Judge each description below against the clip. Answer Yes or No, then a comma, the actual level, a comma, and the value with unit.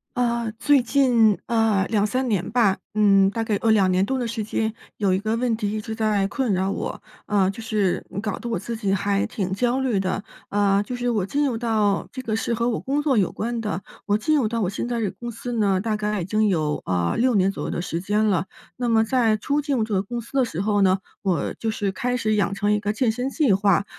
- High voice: Yes, high, 215 Hz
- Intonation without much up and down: No, average, 3.1 semitones